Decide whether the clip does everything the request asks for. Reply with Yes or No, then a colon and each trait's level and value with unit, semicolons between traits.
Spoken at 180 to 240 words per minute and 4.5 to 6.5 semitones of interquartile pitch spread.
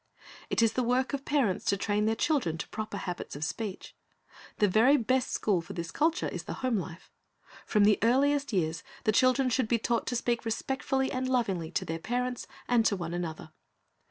Yes: average, 200 wpm; average, 5.1 semitones